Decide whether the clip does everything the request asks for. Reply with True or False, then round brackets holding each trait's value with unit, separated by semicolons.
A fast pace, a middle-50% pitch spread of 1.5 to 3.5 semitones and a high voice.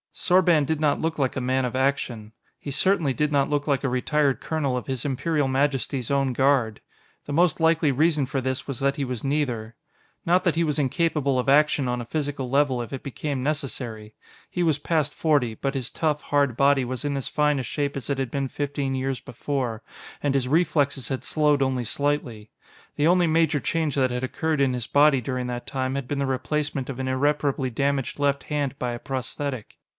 False (210 wpm; 2.4 semitones; 140 Hz)